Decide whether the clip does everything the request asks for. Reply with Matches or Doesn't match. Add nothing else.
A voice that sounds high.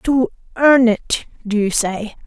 Matches